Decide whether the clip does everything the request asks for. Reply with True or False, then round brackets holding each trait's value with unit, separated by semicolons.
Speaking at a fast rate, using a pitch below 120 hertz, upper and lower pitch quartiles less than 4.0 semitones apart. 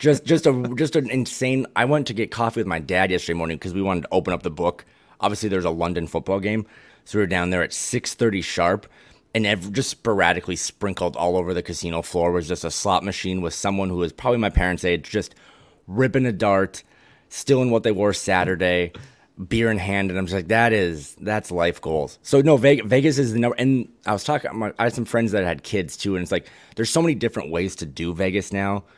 False (235 wpm; 100 Hz; 4.8 semitones)